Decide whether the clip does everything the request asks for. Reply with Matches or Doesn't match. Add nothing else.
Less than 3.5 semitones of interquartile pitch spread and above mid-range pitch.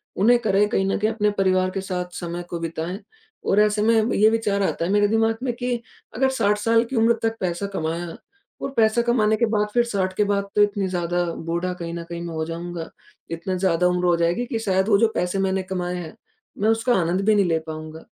Doesn't match